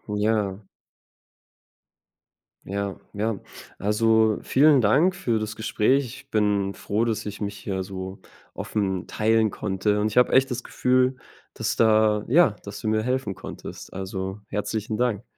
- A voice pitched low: Yes, low, 110 Hz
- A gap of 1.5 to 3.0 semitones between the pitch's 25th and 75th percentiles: Yes, narrow, 2.4 semitones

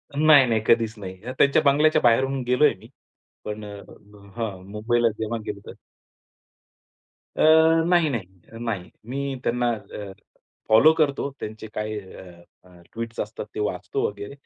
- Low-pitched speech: Yes, low, 115 Hz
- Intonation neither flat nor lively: Yes, average, 4.6 semitones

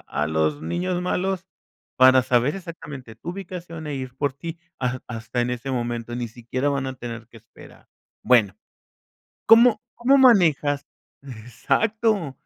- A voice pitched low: Yes, low, 130 Hz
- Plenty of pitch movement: Yes, wide, 6.6 semitones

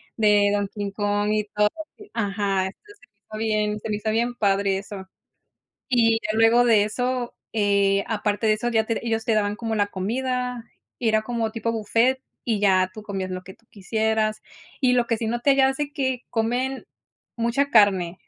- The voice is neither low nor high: No, high, 220 Hz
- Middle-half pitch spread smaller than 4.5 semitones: Yes, average, 2.7 semitones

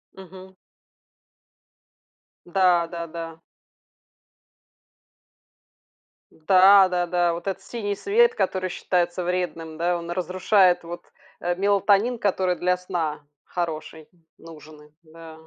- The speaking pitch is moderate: Yes, medium, 180 Hz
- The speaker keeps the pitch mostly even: Yes, narrow, 2.2 semitones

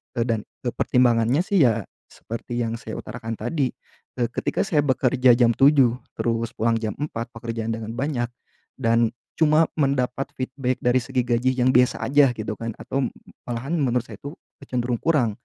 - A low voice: Yes, low, 125 Hz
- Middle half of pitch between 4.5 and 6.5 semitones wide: No, average, 2.7 semitones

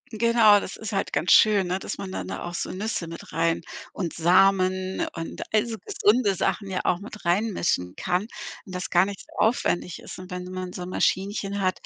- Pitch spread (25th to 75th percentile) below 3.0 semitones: Yes, narrow, 2.6 semitones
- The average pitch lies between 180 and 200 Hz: Yes, high, 190 Hz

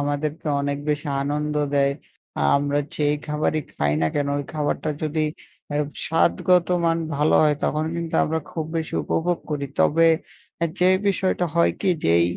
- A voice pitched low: No, medium, 150 Hz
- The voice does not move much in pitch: Yes, narrow, 2.3 semitones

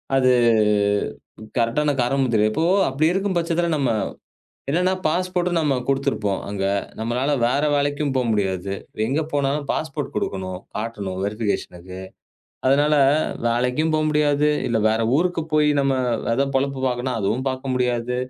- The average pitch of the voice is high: No, low, 135 Hz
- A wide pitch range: No, average, 4.5 semitones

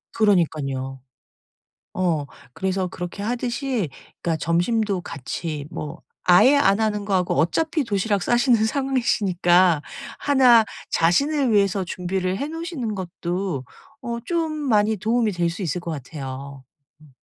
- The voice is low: No, high, 195 Hz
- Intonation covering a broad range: Yes, wide, 5.7 semitones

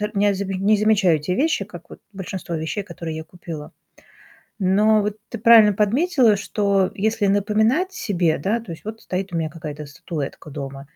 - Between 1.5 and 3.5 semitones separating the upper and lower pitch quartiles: No, average, 4.2 semitones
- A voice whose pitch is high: Yes, high, 195 Hz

